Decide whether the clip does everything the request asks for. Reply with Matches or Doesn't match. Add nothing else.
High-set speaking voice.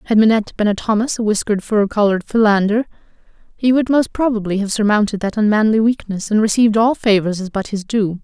Matches